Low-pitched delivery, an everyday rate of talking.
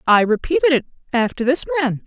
No: high, 230 Hz; average, 175 wpm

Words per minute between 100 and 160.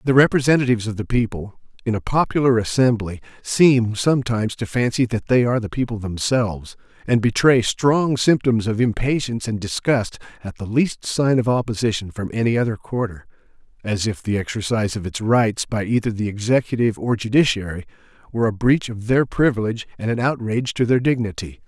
No: average, 170 wpm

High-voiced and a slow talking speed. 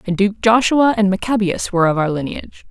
No: high, 200 Hz; average, 200 wpm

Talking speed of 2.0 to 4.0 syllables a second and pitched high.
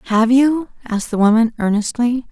No: 5.4 syllables/s; high, 235 Hz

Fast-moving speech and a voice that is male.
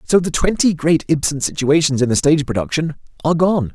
No: average, 190 wpm; male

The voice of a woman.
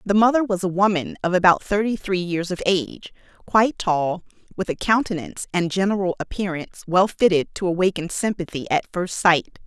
Yes: female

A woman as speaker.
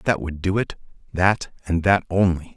No: male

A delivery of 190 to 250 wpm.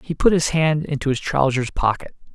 Yes: fast, 205 wpm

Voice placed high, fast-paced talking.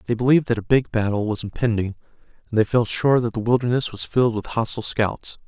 No: low, 115 Hz; fast, 220 wpm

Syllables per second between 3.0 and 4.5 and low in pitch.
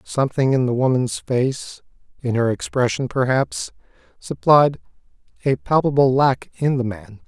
Yes: 4.4 syllables/s; low, 130 Hz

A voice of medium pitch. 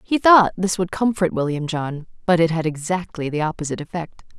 Yes: medium, 170 Hz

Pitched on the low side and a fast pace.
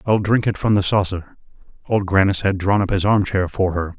Yes: very low, 95 Hz; fast, 225 wpm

